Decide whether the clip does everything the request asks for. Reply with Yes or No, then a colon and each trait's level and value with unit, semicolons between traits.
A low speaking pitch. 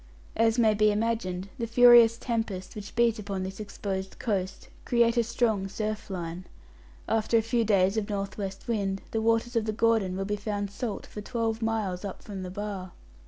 No: high, 210 Hz